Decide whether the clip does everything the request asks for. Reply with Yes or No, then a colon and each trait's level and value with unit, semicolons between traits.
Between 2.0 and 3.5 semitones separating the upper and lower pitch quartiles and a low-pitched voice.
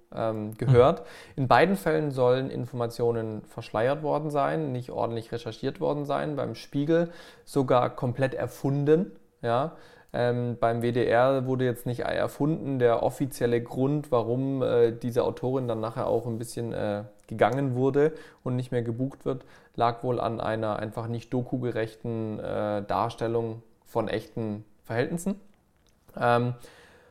Yes: average, 3.2 semitones; low, 120 Hz